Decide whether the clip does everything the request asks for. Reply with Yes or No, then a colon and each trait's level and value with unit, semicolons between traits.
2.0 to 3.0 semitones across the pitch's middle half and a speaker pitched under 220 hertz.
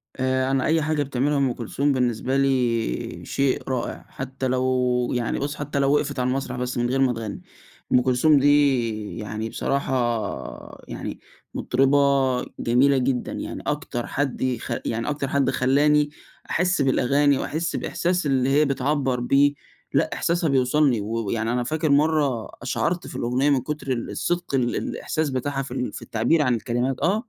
Yes: narrow, 2.5 semitones; low, 135 Hz